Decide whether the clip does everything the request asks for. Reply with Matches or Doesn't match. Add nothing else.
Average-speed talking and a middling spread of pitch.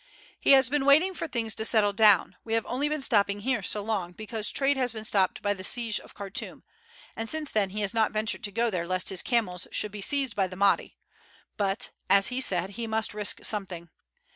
Doesn't match